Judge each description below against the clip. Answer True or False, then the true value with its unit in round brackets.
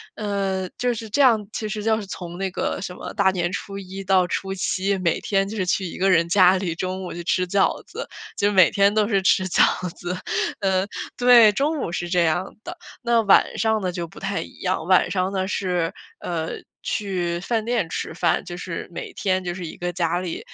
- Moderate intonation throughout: False (2.3 semitones)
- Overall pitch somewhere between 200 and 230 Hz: False (190 Hz)